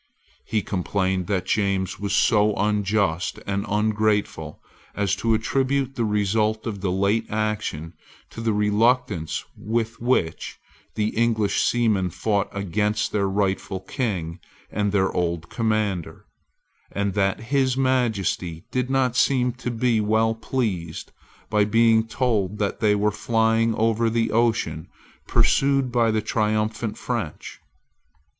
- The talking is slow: Yes, slow, 130 wpm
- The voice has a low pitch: Yes, low, 105 Hz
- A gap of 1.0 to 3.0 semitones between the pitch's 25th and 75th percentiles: Yes, narrow, 2.5 semitones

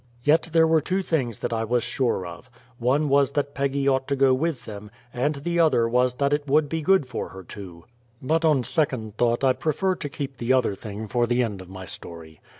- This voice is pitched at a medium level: No, low, 130 Hz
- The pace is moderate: No, fast, 230 wpm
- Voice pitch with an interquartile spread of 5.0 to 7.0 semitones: No, average, 4.3 semitones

